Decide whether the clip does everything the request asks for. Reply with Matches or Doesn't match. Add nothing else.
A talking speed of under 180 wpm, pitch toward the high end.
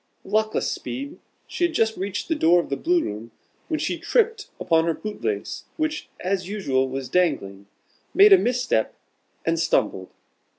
Matches